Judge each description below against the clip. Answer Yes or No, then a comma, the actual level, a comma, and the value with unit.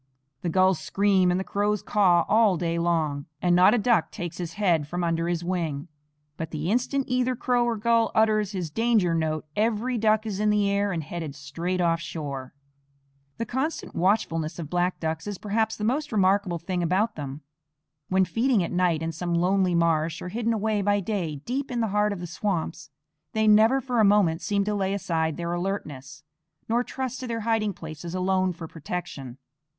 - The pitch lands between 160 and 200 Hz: Yes, medium, 185 Hz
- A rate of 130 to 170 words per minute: No, average, 195 wpm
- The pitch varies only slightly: No, average, 4.3 semitones